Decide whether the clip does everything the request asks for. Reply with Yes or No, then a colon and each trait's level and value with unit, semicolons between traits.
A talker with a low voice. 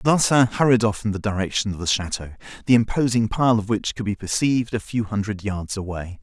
Yes: low, 110 Hz